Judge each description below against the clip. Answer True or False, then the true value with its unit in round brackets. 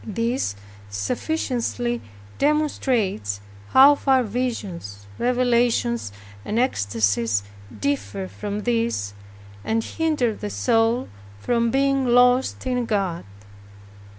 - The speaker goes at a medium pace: False (90 wpm)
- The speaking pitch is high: True (230 Hz)